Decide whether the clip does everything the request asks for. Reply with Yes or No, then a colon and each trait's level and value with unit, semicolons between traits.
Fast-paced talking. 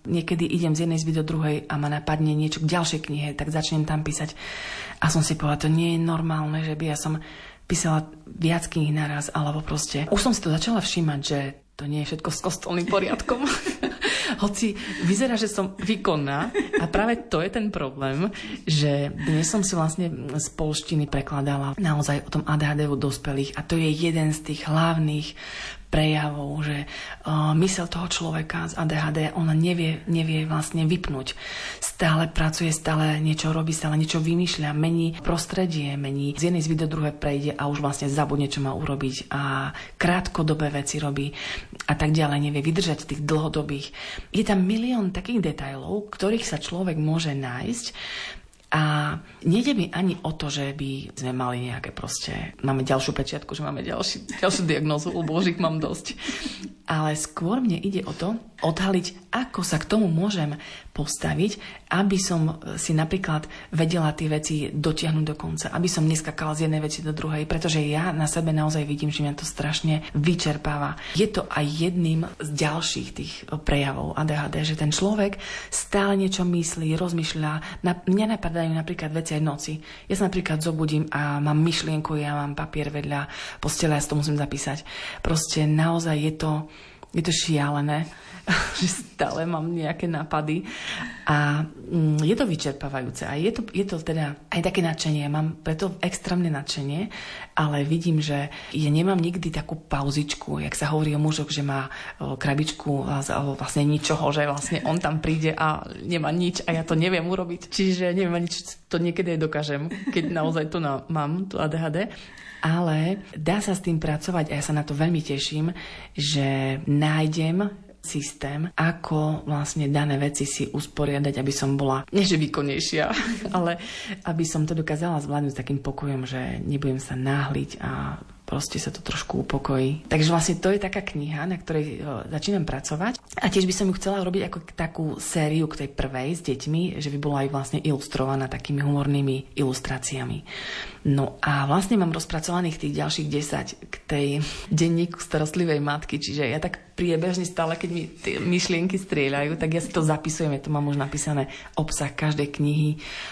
Yes: fast, 170 wpm